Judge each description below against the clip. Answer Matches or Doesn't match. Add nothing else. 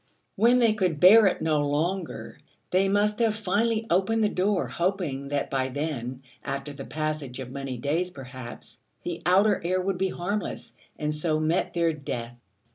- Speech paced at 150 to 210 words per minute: Matches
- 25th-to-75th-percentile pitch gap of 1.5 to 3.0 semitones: Doesn't match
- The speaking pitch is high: Doesn't match